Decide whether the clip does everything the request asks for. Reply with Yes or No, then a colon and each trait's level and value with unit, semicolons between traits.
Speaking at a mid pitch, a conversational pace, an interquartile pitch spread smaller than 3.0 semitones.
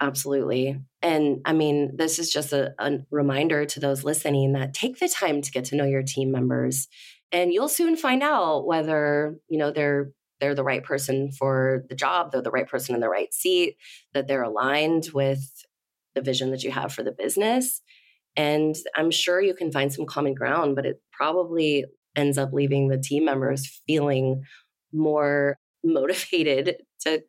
Yes: medium, 145 Hz; average, 180 wpm; narrow, 2.6 semitones